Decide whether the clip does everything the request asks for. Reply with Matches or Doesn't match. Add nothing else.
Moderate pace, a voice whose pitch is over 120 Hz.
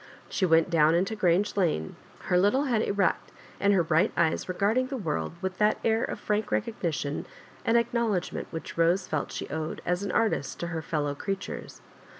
Matches